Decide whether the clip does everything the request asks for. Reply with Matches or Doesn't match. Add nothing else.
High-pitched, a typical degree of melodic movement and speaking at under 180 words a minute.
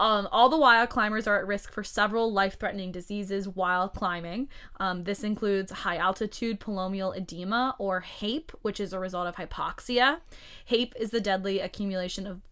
Matches